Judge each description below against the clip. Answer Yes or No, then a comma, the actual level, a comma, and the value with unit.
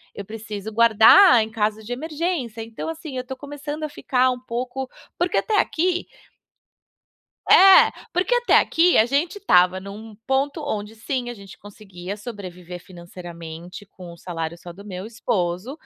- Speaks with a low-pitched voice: No, high, 225 Hz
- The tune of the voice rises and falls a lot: Yes, wide, 6.7 semitones